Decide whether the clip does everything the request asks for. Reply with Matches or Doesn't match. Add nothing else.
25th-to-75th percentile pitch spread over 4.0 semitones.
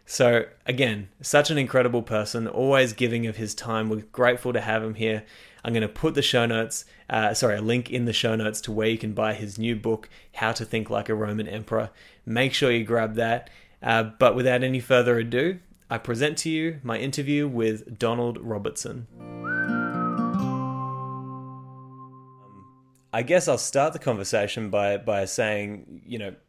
Doesn't match